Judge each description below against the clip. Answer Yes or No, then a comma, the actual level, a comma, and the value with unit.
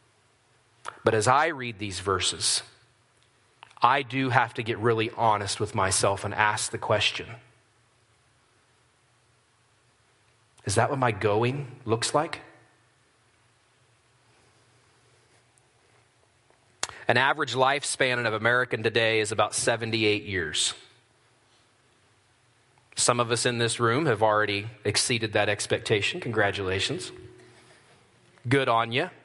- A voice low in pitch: Yes, low, 120 Hz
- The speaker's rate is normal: No, slow, 105 wpm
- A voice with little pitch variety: Yes, narrow, 2.0 semitones